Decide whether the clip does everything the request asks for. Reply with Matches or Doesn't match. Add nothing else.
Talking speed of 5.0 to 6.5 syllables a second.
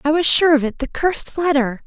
Matches